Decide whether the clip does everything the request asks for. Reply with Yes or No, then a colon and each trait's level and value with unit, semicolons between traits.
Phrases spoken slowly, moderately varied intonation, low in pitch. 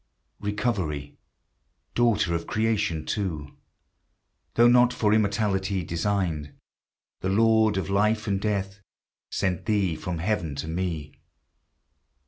Yes: slow, 110 wpm; average, 4.2 semitones; low, 100 Hz